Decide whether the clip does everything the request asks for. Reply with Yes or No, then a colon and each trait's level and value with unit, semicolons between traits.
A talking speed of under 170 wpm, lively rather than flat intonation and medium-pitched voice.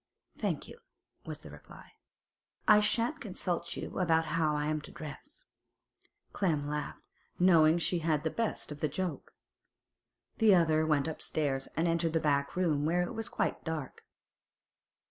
No: average, 150 wpm; average, 3.1 semitones; medium, 160 Hz